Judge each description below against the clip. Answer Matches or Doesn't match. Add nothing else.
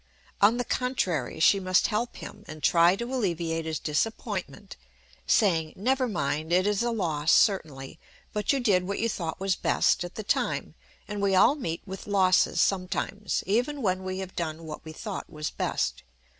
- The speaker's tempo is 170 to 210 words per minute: Matches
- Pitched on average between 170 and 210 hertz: Matches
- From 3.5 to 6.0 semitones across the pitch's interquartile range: Matches